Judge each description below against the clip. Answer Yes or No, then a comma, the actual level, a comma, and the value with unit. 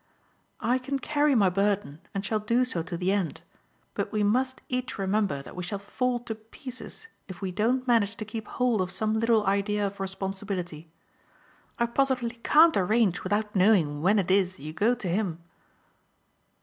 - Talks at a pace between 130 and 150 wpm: No, average, 175 wpm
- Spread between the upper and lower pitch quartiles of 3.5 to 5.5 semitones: Yes, average, 4.0 semitones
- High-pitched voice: Yes, high, 210 Hz